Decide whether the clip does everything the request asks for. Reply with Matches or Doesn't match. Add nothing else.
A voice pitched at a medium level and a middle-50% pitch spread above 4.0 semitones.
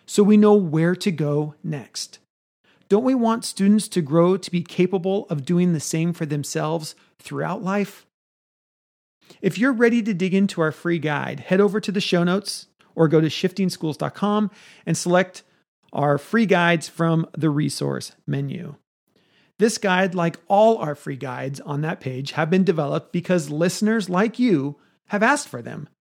Matches